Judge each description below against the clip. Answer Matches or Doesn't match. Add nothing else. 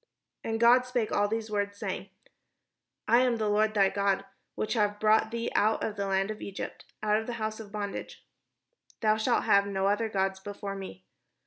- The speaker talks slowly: Doesn't match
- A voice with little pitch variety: Matches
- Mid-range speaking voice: Doesn't match